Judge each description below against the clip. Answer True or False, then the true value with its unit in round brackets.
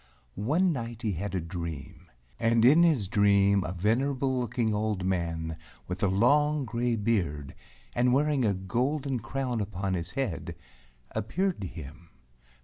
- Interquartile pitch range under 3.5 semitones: False (5.5 semitones)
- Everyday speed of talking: True (145 wpm)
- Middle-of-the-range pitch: False (110 Hz)